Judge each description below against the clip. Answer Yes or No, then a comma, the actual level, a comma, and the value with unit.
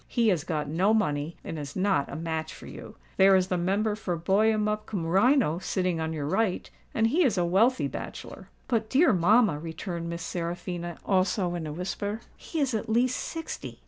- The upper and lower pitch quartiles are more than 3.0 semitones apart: Yes, average, 4.7 semitones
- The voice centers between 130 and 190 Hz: Yes, medium, 185 Hz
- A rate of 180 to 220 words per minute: Yes, average, 195 wpm